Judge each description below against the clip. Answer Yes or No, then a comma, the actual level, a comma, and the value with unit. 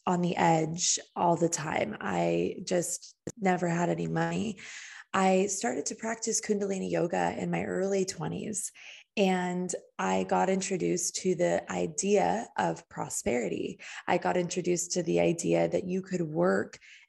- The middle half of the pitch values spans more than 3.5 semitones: No, narrow, 2.5 semitones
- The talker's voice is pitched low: No, medium, 180 Hz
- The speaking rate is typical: Yes, average, 145 wpm